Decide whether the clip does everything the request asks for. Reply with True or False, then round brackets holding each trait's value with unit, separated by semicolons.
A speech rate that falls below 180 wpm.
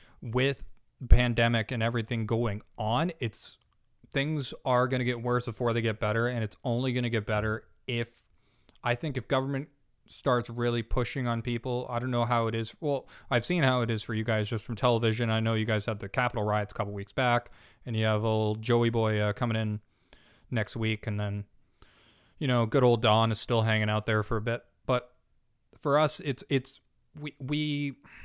False (205 wpm)